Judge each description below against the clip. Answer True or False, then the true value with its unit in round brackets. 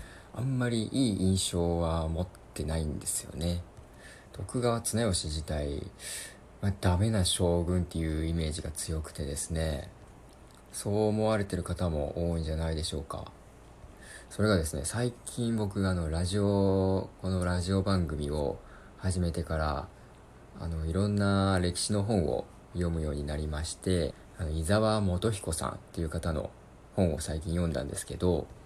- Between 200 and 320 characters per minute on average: True (300 characters per minute)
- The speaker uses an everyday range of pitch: True (3.8 semitones)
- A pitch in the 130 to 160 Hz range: False (90 Hz)